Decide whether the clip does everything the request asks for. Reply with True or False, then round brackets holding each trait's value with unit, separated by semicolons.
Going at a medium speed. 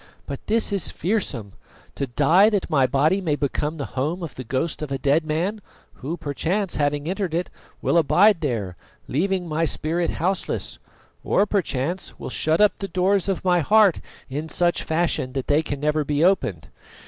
True (180 wpm)